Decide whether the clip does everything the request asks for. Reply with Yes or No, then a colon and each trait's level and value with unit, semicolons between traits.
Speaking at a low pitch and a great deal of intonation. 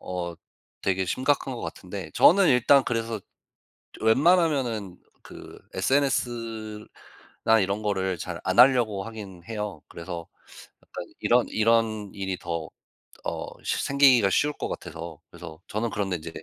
No: low, 110 Hz; average, 4.7 semitones